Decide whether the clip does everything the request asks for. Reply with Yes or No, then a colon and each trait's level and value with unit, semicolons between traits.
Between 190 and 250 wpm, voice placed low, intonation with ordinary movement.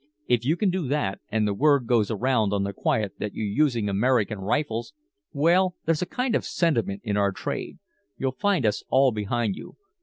No: fast, 205 wpm; low, 120 Hz; wide, 6.4 semitones